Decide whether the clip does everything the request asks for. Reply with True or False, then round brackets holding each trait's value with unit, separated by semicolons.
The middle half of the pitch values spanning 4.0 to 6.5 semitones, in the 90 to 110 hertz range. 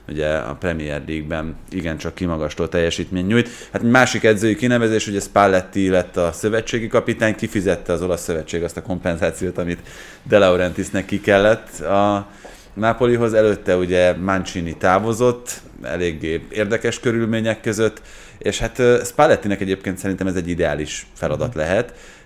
True (4.3 semitones; 95 Hz)